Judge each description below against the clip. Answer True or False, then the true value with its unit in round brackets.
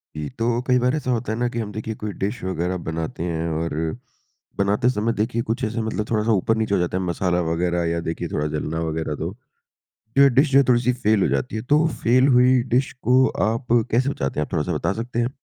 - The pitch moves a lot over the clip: True (6.0 semitones)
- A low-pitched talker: True (110 Hz)